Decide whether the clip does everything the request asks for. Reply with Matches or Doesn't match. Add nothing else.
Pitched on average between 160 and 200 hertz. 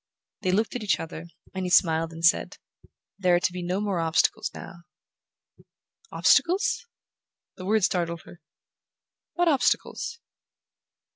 Matches